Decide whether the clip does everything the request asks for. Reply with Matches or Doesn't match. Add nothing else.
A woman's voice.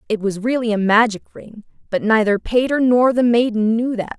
Matches